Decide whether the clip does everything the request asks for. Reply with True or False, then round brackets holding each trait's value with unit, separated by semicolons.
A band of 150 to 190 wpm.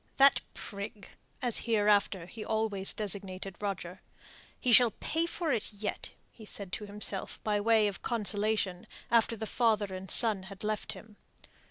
True (155 wpm)